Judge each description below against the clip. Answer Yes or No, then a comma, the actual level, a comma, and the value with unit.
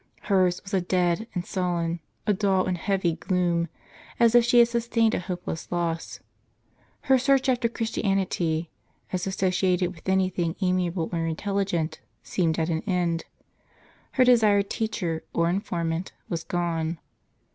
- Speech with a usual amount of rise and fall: Yes, average, 3.1 semitones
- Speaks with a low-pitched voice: No, medium, 180 Hz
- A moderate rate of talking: Yes, average, 145 wpm